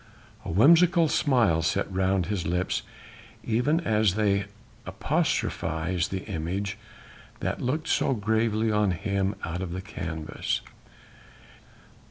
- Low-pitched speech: Yes, low, 100 Hz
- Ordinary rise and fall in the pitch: Yes, average, 3.8 semitones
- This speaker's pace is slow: Yes, slow, 115 wpm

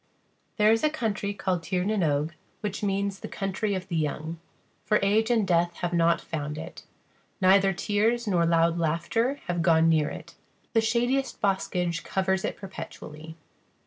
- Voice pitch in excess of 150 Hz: Yes, high, 190 Hz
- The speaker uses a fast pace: No, average, 170 wpm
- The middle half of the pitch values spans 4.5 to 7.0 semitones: No, average, 3.9 semitones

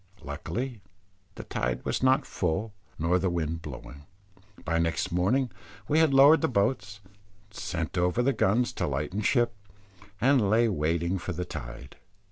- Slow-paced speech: No, average, 155 wpm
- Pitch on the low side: Yes, very low, 95 Hz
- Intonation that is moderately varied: No, wide, 6.7 semitones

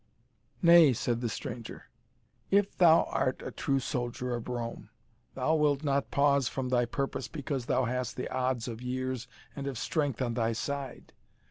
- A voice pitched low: Yes, low, 130 Hz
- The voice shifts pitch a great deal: No, narrow, 2.6 semitones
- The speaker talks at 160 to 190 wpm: Yes, average, 165 wpm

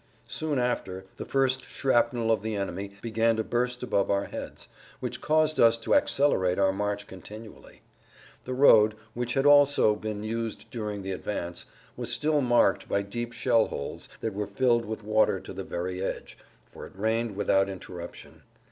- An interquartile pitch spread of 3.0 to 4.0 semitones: Yes, average, 3.6 semitones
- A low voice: Yes, low, 110 Hz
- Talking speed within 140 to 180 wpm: Yes, average, 170 wpm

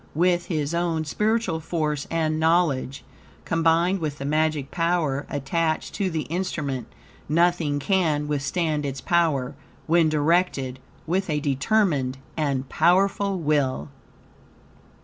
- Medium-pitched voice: Yes, medium, 155 Hz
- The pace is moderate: No, slow, 115 wpm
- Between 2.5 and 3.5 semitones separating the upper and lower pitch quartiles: Yes, average, 3.2 semitones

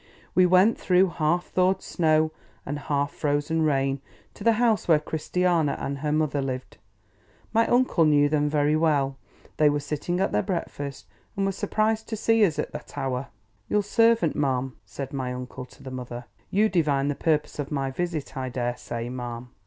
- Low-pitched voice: No, medium, 150 Hz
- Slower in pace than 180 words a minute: No, average, 185 wpm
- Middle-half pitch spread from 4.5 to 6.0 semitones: Yes, average, 4.9 semitones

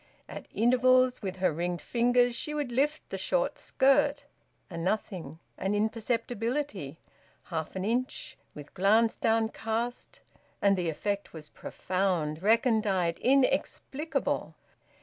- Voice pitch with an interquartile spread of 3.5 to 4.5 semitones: No, average, 5.3 semitones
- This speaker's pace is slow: Yes, slow, 115 wpm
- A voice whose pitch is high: Yes, high, 220 Hz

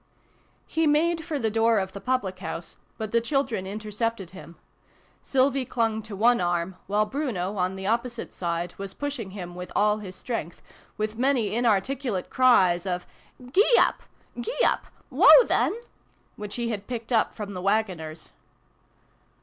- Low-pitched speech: No, high, 215 Hz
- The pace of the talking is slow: No, average, 165 wpm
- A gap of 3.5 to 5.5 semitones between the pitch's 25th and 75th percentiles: Yes, average, 4.7 semitones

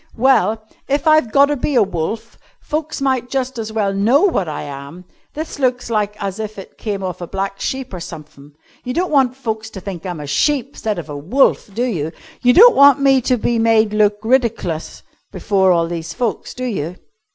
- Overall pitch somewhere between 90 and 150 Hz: No, high, 220 Hz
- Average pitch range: No, wide, 5.9 semitones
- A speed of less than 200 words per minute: No, fast, 205 wpm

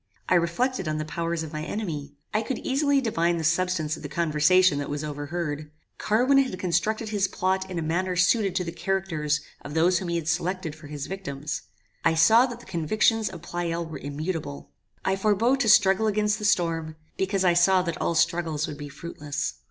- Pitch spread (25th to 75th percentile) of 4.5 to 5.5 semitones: No, average, 3.8 semitones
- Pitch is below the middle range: No, medium, 175 Hz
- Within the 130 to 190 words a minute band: No, average, 200 wpm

